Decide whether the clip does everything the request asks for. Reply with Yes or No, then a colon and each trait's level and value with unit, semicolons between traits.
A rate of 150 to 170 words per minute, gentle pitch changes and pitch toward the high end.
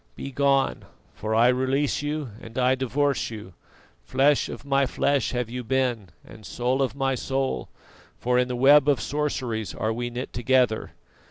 No: average, 165 wpm; narrow, 2.2 semitones; low, 130 Hz